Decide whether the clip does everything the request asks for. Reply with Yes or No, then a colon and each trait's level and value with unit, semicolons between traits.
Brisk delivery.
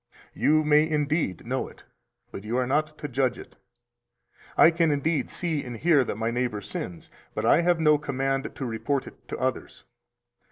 No: average, 185 wpm